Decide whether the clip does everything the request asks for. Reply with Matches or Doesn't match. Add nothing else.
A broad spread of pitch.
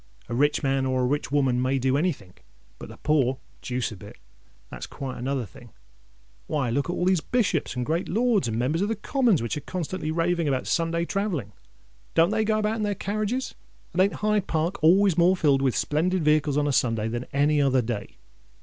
Matches